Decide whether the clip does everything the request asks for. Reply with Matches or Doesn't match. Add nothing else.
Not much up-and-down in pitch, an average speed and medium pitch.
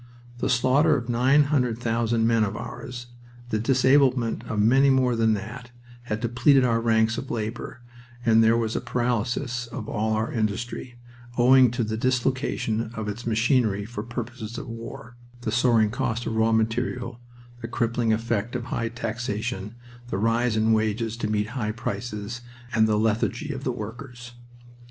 Doesn't match